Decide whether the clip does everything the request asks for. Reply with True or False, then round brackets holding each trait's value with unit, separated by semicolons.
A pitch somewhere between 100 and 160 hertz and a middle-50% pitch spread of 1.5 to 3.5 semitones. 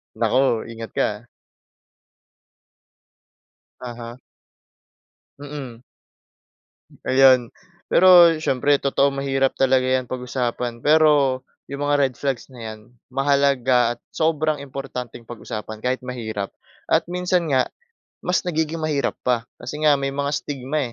True (135 Hz; 2.9 semitones)